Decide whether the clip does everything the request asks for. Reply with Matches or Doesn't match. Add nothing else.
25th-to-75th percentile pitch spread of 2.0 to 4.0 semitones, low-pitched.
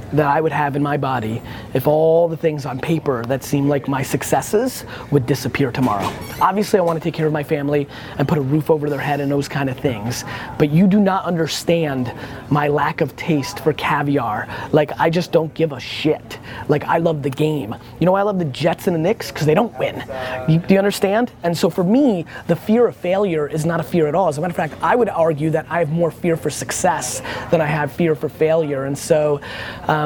Doesn't match